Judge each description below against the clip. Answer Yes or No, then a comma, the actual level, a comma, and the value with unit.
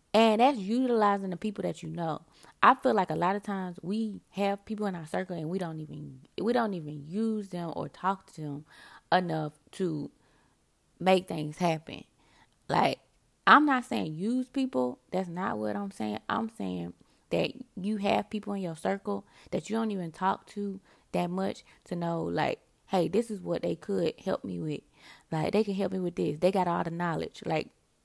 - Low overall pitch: No, medium, 185 Hz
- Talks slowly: No, average, 195 wpm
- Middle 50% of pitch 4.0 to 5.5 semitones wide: Yes, average, 4.5 semitones